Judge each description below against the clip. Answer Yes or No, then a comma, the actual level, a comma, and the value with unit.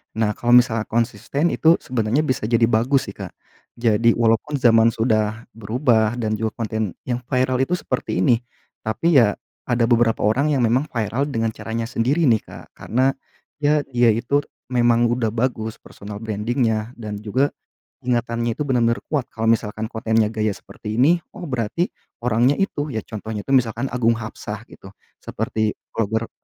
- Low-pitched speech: Yes, low, 115 Hz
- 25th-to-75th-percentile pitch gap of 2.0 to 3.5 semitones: Yes, narrow, 2.6 semitones